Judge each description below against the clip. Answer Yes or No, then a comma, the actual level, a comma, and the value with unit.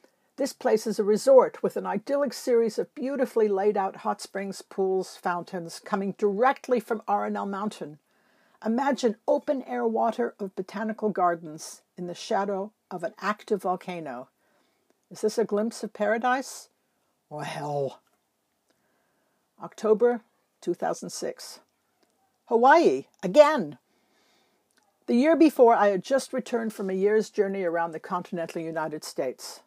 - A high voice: Yes, high, 215 Hz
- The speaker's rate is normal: No, slow, 130 wpm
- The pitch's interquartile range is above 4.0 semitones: Yes, average, 5.0 semitones